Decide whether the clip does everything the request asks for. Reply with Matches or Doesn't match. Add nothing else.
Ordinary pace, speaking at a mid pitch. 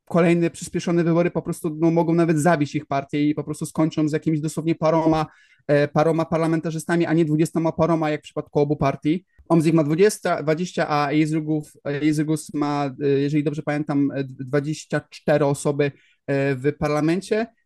Matches